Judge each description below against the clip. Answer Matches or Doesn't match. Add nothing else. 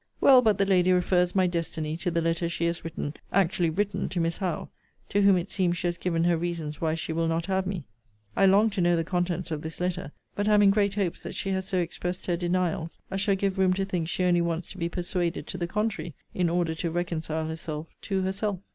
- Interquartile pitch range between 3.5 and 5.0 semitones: Doesn't match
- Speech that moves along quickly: Matches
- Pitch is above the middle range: Doesn't match